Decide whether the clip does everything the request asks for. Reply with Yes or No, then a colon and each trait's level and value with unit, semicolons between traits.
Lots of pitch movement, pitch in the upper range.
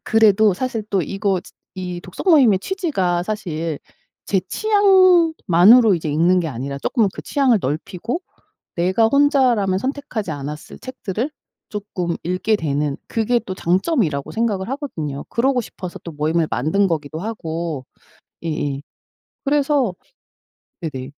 Yes: wide, 7.1 semitones; high, 195 Hz